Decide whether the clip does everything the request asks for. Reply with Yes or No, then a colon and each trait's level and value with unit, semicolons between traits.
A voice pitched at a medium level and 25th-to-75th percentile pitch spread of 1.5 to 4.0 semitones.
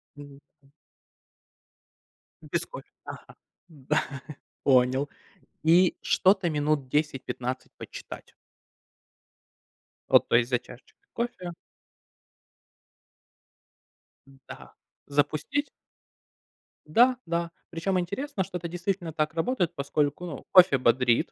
No: medium, 160 Hz; average, 4.6 semitones